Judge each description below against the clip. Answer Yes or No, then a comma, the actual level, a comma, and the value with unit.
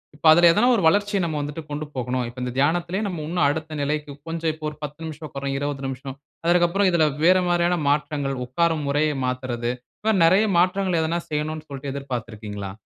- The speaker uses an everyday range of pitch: Yes, average, 3.9 semitones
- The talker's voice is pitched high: No, medium, 155 Hz